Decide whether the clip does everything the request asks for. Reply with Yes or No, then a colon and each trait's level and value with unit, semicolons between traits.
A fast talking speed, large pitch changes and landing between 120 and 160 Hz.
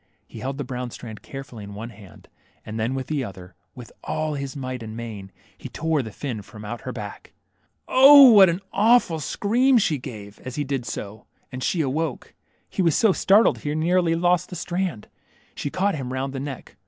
Yes: fast, 215 wpm; wide, 6.7 semitones; low, 135 Hz